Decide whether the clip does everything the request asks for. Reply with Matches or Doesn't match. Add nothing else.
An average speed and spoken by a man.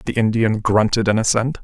Matches